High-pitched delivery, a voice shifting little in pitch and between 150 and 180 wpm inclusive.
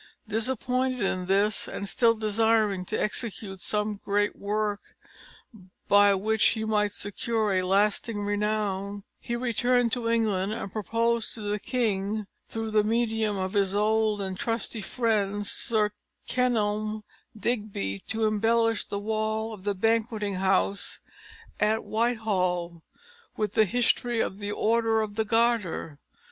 No: high, 215 Hz; narrow, 1.9 semitones; slow, 135 wpm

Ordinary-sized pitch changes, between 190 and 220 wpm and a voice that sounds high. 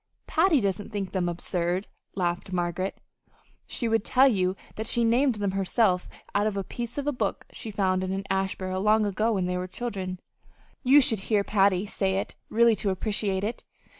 Yes: average, 3.3 semitones; average, 195 wpm; high, 200 Hz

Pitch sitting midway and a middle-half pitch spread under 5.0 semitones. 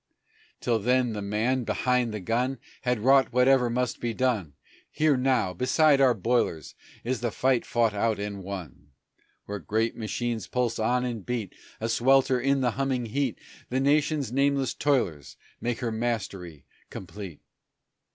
No: low, 120 Hz; average, 3.5 semitones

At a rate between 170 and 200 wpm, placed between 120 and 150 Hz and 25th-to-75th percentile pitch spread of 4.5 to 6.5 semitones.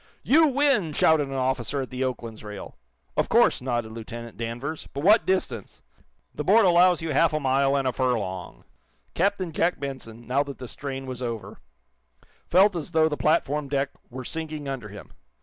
Yes: average, 180 wpm; medium, 140 Hz; average, 4.9 semitones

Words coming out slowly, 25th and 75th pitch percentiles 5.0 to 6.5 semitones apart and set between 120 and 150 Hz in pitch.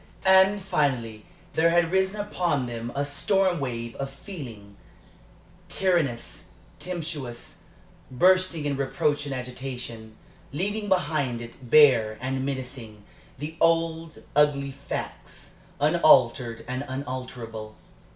Yes: slow, 105 wpm; average, 5.3 semitones; medium, 140 Hz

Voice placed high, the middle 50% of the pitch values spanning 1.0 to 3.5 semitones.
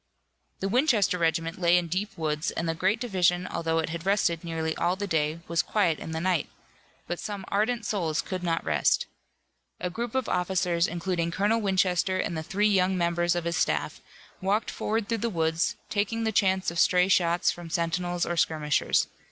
No: medium, 180 Hz; average, 2.9 semitones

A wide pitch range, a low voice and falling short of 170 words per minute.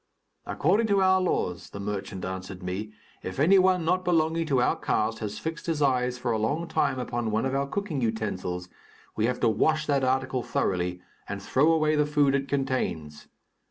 No: wide, 6.8 semitones; low, 130 Hz; average, 195 wpm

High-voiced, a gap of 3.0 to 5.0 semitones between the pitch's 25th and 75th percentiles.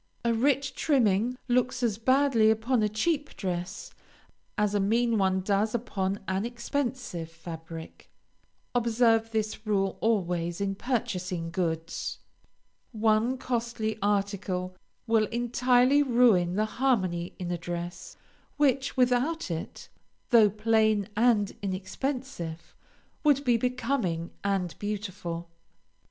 Yes: high, 215 Hz; average, 4.6 semitones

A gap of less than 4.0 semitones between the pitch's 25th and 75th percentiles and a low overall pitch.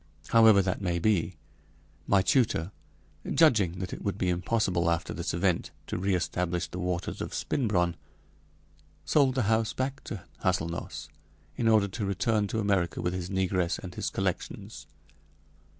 Yes: average, 3.6 semitones; very low, 95 Hz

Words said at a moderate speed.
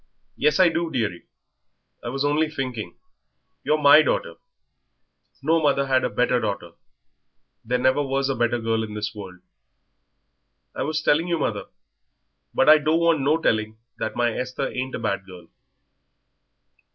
Yes: average, 160 wpm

